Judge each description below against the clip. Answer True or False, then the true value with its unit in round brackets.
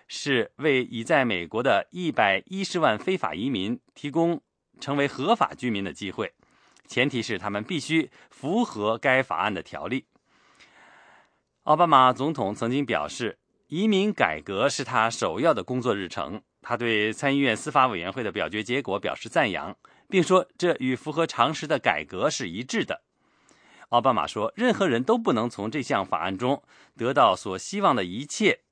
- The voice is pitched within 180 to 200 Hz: False (140 Hz)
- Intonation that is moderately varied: False (7.1 semitones)